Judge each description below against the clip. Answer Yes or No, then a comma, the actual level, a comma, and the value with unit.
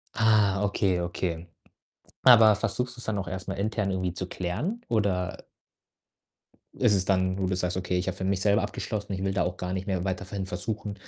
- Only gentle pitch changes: Yes, narrow, 2.2 semitones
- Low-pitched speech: Yes, very low, 95 Hz